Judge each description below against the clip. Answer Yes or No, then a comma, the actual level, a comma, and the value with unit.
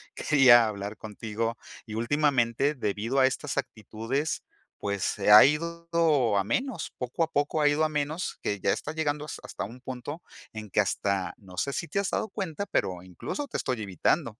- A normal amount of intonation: No, wide, 6.1 semitones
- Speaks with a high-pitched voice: No, low, 130 Hz